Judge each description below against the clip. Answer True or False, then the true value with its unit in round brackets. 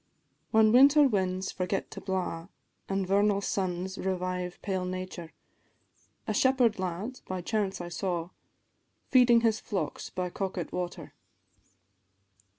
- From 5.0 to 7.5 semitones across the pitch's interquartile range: False (2.7 semitones)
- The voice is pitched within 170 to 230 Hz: True (190 Hz)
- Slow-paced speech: True (125 wpm)